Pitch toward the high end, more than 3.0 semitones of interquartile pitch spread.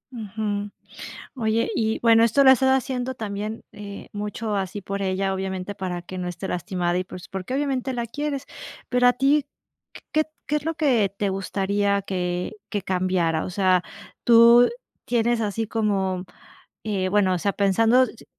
Yes: high, 205 Hz; average, 3.9 semitones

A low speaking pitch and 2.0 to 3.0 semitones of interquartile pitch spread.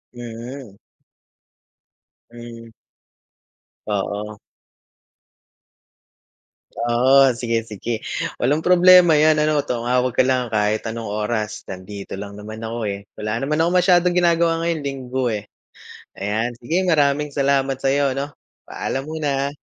No: low, 125 Hz; average, 4.8 semitones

